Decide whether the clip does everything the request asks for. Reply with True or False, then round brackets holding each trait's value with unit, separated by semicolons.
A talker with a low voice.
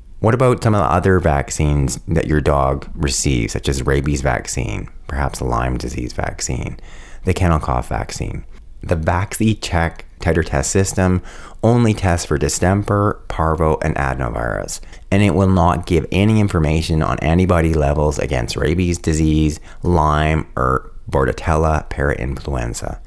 True (80 Hz)